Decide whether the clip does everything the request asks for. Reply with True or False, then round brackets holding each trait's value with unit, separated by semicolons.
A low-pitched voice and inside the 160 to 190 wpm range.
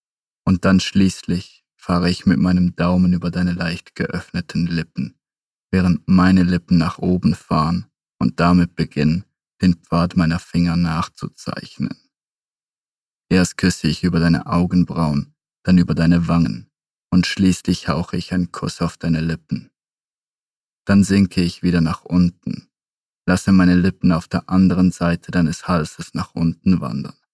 False (90 Hz; 140 wpm)